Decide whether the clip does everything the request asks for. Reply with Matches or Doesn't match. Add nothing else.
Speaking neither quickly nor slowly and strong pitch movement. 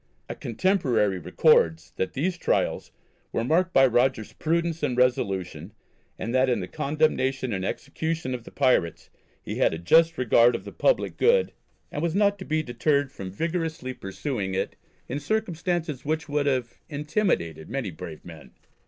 Matches